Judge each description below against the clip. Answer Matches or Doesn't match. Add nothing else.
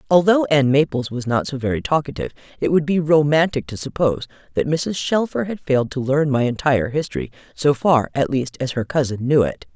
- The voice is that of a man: Doesn't match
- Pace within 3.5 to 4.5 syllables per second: Doesn't match